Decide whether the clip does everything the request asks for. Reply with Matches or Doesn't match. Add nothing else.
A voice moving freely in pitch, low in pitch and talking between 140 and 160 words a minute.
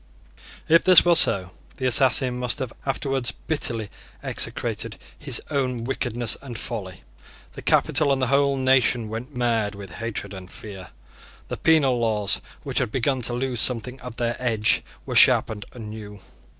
Doesn't match